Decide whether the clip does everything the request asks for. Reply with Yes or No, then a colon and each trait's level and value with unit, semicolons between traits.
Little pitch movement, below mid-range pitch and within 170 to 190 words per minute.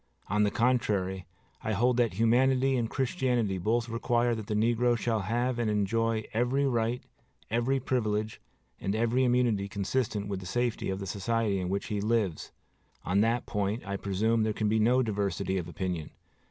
No: average, 3.2 semitones; low, 110 Hz; average, 175 wpm